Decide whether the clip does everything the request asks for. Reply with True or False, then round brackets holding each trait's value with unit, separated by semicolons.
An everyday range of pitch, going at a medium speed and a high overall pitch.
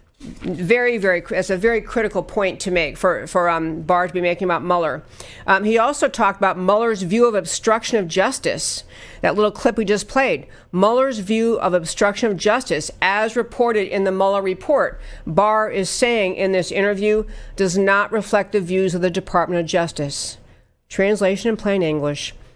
True (3.4 semitones; 180 wpm; 195 Hz)